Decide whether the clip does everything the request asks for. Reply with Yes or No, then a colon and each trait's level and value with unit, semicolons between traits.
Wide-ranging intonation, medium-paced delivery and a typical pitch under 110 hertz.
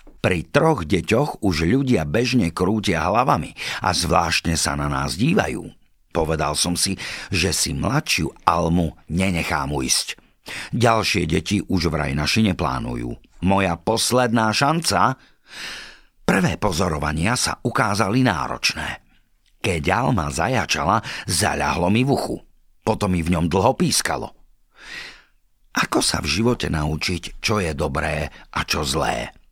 Yes: wide, 6.1 semitones; average, 125 wpm; very low, 90 Hz